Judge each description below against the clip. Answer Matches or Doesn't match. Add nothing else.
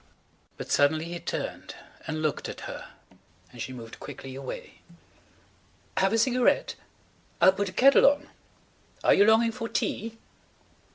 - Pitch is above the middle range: Matches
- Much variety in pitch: Matches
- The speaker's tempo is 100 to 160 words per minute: Matches